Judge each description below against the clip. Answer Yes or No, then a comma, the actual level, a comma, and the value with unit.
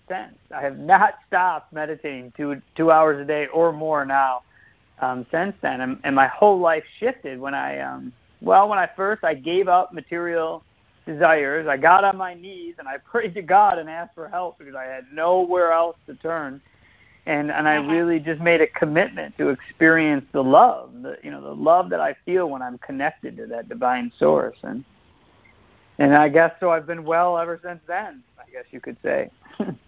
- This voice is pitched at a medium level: Yes, medium, 160 Hz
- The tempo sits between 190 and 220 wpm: Yes, average, 200 wpm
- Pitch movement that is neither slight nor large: Yes, average, 4.3 semitones